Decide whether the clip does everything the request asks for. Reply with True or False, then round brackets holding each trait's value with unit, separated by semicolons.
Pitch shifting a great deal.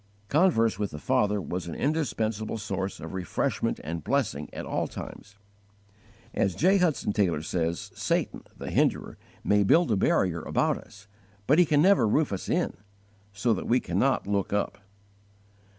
True (6.5 semitones)